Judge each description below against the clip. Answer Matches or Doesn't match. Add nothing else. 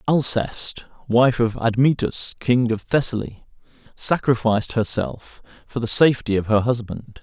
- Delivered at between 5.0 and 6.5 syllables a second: Doesn't match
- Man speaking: Matches